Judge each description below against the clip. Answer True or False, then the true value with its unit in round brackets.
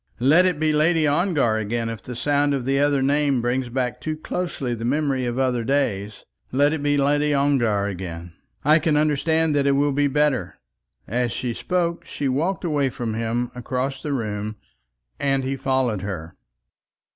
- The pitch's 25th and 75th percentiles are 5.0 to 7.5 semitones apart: False (3.6 semitones)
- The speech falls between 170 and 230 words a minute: True (180 wpm)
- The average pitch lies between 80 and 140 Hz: True (135 Hz)